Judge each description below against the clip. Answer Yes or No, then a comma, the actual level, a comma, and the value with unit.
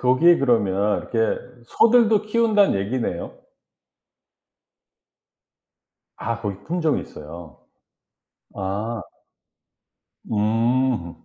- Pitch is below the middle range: Yes, low, 115 Hz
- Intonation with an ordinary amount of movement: No, wide, 8.4 semitones